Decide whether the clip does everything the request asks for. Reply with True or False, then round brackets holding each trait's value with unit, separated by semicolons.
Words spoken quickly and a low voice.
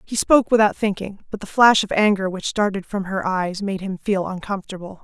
False (215 wpm; 200 Hz)